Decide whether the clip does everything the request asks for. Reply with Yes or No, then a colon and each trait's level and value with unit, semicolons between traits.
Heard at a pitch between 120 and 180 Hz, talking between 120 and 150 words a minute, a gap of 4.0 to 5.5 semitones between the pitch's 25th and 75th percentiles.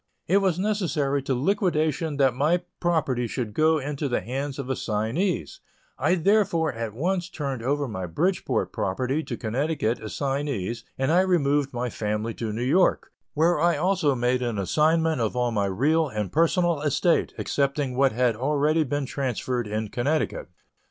No: medium, 140 Hz; average, 160 wpm; average, 4.9 semitones